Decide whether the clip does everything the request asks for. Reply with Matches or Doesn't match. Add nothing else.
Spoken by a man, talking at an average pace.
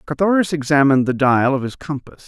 Matches